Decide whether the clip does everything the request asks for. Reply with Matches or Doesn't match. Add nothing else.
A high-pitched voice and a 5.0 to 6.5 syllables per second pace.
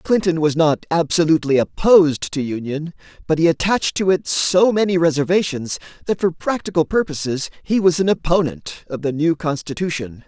Doesn't match